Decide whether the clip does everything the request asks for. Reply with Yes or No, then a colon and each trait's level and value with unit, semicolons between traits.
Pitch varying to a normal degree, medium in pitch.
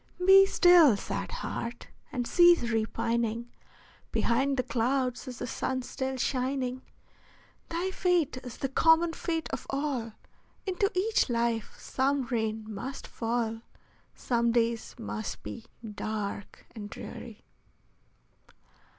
No: average, 3.7 semitones; very high, 250 Hz